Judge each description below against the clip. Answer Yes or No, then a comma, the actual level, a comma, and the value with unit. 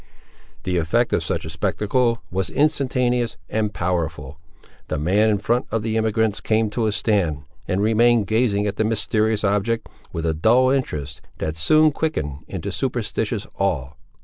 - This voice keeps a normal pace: Yes, average, 160 wpm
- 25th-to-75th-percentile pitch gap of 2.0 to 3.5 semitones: No, average, 4.8 semitones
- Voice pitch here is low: Yes, low, 105 Hz